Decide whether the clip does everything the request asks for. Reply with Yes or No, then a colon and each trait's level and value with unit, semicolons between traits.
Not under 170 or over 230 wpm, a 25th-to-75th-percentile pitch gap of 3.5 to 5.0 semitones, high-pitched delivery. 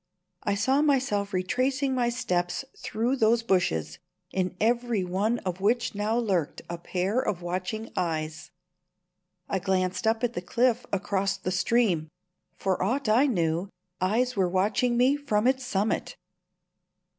No: average, 145 wpm; average, 4.7 semitones; high, 205 Hz